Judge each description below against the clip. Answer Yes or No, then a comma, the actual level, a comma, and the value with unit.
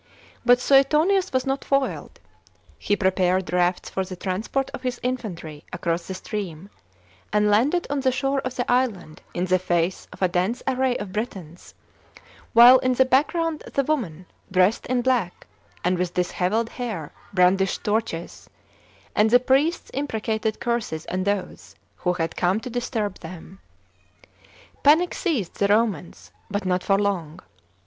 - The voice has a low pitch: No, high, 210 Hz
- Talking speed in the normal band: Yes, average, 150 wpm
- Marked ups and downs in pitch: Yes, wide, 5.9 semitones